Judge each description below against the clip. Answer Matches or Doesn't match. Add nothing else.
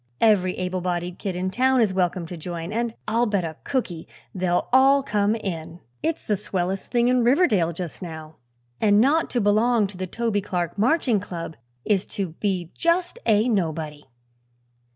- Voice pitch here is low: Doesn't match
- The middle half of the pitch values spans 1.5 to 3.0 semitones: Doesn't match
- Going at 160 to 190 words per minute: Matches